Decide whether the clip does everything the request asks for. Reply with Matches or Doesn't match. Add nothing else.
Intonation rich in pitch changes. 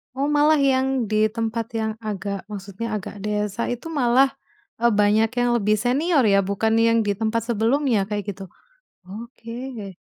Doesn't match